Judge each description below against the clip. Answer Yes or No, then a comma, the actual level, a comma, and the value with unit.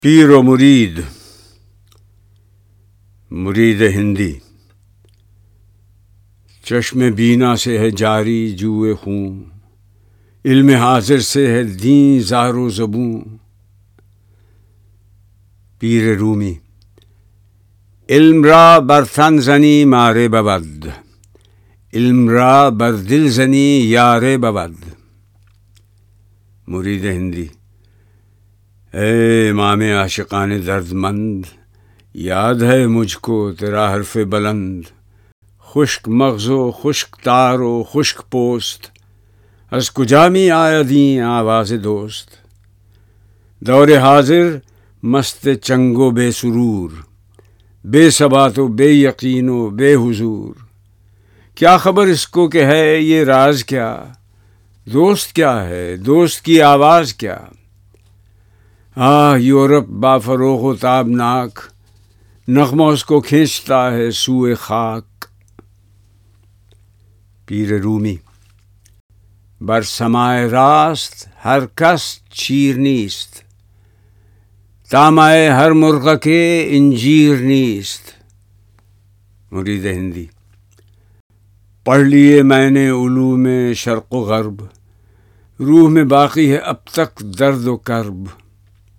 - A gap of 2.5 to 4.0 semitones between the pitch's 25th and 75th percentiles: No, average, 4.7 semitones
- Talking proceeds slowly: Yes, slow, 95 wpm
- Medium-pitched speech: No, low, 110 Hz